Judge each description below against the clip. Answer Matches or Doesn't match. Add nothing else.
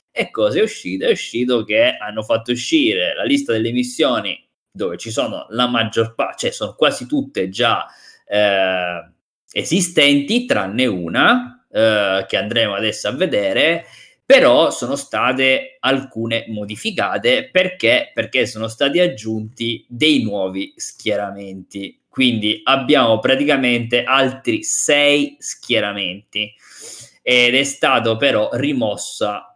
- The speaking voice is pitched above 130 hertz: Doesn't match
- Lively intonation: Matches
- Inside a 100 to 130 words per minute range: Matches